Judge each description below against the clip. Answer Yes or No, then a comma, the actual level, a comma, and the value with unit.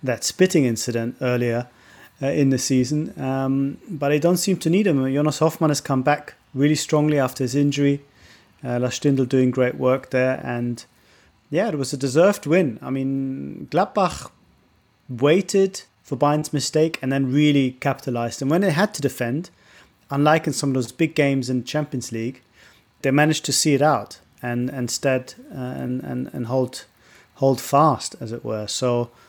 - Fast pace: No, average, 175 wpm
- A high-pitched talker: No, low, 135 Hz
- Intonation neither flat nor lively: Yes, average, 3.1 semitones